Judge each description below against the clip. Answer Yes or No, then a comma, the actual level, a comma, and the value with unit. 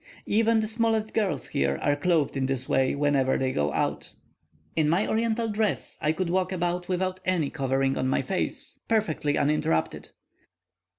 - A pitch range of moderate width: No, wide, 7.3 semitones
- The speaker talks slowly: No, average, 165 wpm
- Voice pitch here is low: No, medium, 165 Hz